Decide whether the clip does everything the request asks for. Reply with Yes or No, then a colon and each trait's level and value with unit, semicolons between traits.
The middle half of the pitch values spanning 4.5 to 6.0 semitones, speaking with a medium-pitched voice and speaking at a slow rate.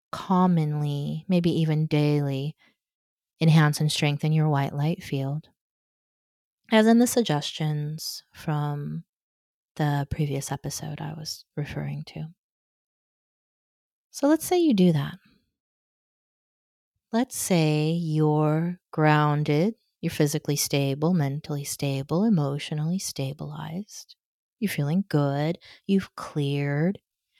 No: average, 3.2 semitones; medium, 155 Hz; slow, 100 wpm